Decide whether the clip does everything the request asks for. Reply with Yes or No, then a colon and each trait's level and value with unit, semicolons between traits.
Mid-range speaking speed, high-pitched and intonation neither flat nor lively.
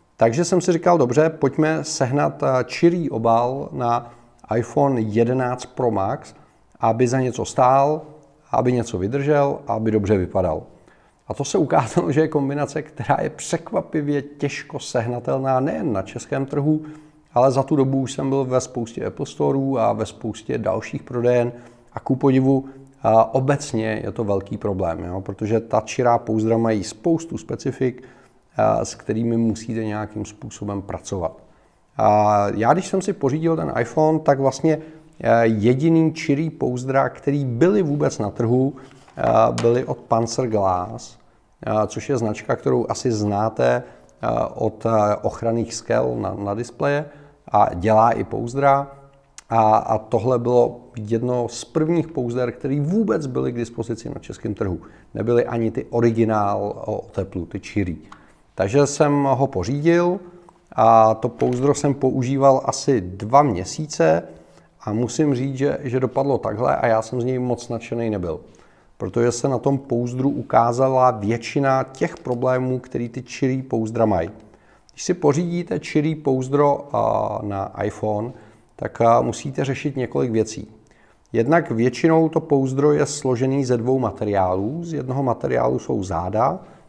No: average, 140 wpm; low, 125 Hz; average, 4.2 semitones